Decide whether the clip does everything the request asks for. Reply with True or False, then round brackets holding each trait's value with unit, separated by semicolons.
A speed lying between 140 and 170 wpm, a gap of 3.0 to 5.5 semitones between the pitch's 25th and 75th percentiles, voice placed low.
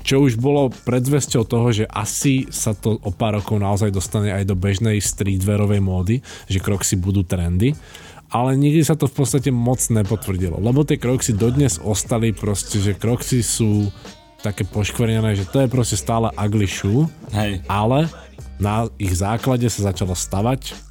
True (160 wpm; 3.7 semitones; 110 Hz)